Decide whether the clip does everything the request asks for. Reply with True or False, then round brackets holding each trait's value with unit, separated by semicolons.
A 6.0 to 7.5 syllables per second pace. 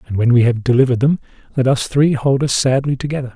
True (6.8 syllables/s)